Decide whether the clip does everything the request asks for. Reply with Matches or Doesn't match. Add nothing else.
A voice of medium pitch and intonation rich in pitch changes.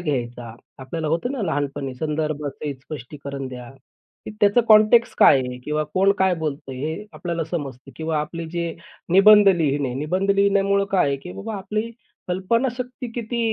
Matches